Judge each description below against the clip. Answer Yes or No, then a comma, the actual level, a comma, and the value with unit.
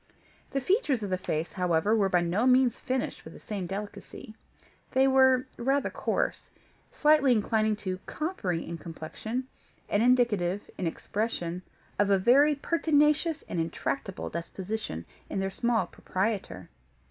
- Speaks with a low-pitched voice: No, high, 215 Hz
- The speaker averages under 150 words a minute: Yes, average, 140 wpm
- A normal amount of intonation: No, wide, 6.1 semitones